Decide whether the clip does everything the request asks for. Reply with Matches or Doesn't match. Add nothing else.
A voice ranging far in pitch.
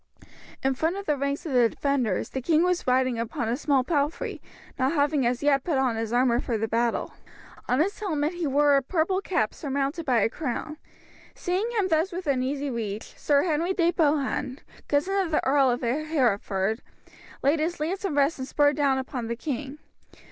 Doesn't match